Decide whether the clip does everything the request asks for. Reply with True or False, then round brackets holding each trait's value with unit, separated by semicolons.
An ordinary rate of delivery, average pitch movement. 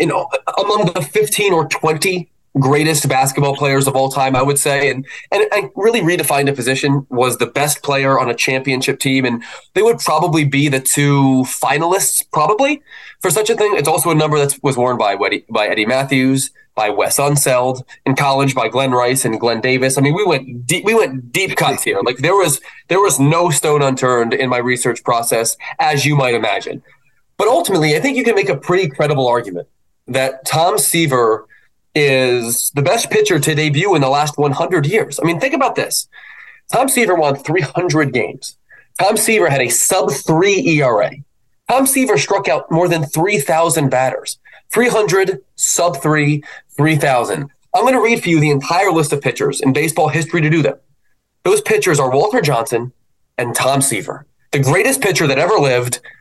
True (190 wpm; 4.8 semitones)